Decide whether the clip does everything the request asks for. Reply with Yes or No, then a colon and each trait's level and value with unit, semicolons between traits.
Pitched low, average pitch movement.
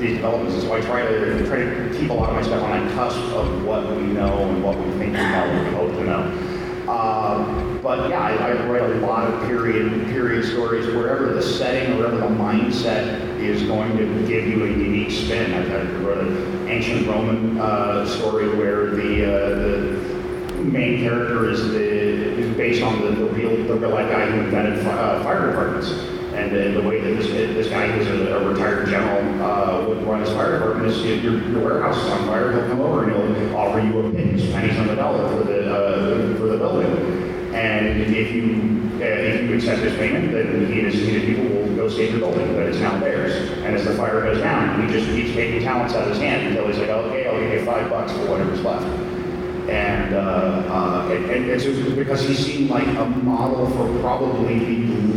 No: low, 110 Hz; narrow, 2.2 semitones